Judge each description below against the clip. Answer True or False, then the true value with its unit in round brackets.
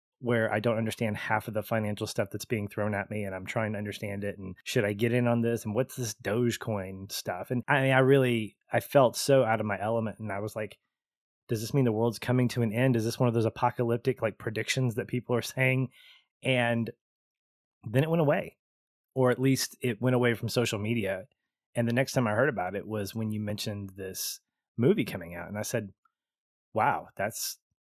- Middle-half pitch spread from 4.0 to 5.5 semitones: False (2.8 semitones)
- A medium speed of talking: False (225 wpm)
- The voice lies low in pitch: True (115 Hz)